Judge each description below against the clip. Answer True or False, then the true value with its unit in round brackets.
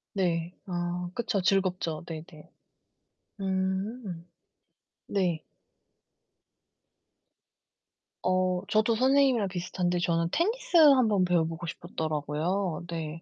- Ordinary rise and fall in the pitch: True (3.4 semitones)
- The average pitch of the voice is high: False (180 Hz)